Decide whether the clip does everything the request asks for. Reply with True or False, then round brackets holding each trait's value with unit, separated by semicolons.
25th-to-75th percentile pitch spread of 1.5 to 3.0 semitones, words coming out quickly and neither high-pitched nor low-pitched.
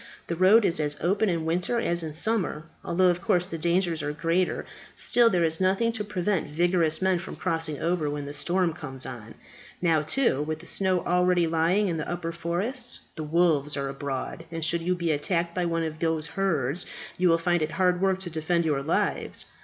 True (2.5 semitones; 210 wpm; 170 Hz)